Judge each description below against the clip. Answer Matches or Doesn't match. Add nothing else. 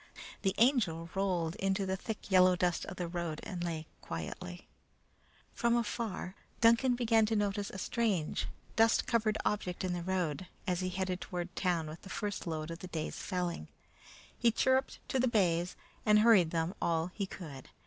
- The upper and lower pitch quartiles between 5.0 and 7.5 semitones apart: Doesn't match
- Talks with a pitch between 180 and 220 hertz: Matches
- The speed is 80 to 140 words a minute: Doesn't match